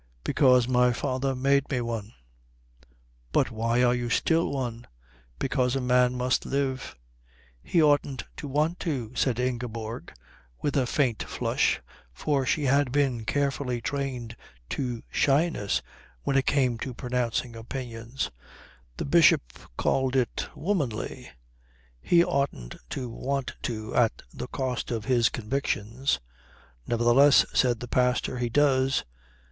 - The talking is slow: Yes, slow, 130 wpm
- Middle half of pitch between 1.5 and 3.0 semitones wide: Yes, narrow, 2.6 semitones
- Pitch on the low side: Yes, low, 125 Hz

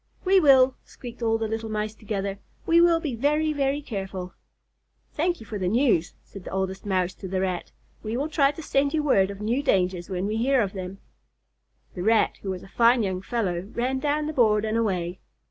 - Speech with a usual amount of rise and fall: No, wide, 6.2 semitones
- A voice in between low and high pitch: No, high, 220 Hz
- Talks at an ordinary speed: No, fast, 215 wpm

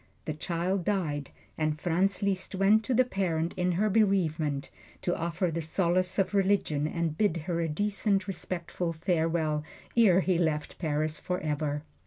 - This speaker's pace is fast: No, average, 155 wpm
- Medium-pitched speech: Yes, medium, 175 Hz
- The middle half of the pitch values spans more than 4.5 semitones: No, average, 3.6 semitones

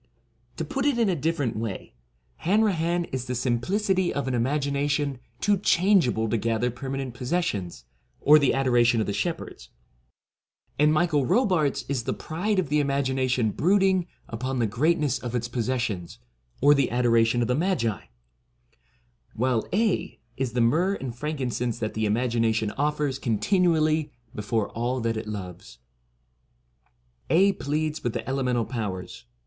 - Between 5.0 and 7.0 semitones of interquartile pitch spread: Yes, average, 5.3 semitones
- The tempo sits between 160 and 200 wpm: No, average, 150 wpm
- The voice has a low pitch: Yes, low, 130 Hz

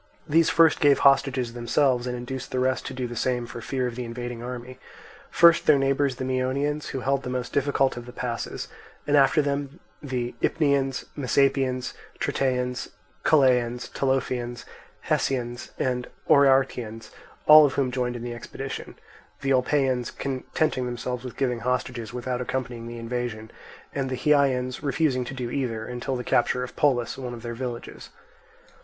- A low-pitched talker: Yes, low, 130 Hz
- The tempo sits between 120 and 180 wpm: Yes, average, 160 wpm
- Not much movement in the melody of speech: Yes, narrow, 1.9 semitones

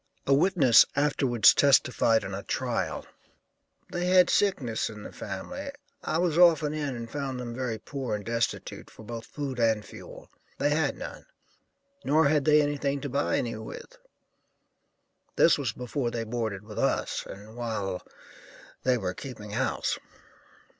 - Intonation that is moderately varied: Yes, average, 4.7 semitones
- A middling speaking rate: Yes, average, 155 wpm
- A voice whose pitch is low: Yes, low, 130 Hz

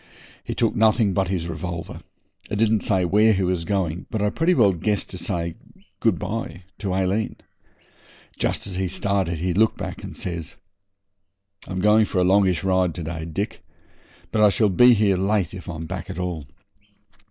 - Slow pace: No, average, 185 wpm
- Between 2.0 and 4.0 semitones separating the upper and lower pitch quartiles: Yes, average, 3.0 semitones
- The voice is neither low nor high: No, very low, 95 Hz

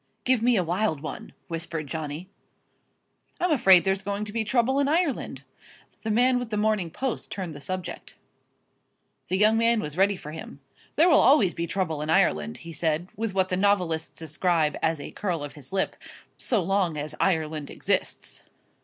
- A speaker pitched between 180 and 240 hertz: Yes, medium, 185 Hz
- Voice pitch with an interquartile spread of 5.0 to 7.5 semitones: Yes, average, 5.3 semitones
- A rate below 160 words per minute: No, average, 180 wpm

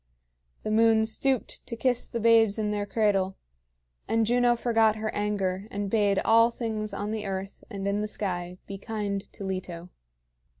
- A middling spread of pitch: No, narrow, 2.3 semitones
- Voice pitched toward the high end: Yes, high, 210 Hz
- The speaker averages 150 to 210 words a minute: Yes, average, 170 wpm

